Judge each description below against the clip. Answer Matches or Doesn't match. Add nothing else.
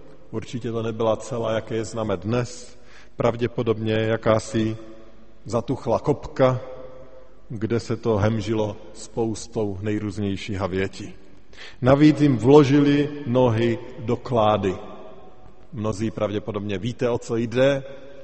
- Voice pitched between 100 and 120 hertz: Matches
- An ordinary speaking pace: Doesn't match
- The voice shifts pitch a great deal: Doesn't match